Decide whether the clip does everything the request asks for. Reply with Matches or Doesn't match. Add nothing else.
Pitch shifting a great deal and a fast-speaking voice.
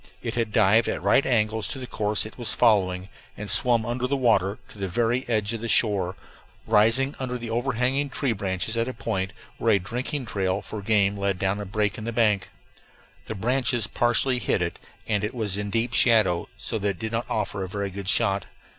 Doesn't match